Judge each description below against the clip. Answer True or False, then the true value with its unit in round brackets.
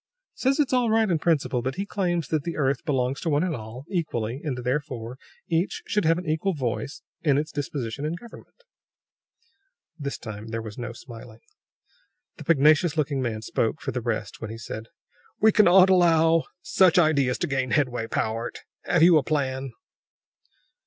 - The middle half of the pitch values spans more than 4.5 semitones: True (5.5 semitones)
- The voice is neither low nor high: True (145 Hz)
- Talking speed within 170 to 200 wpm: True (175 wpm)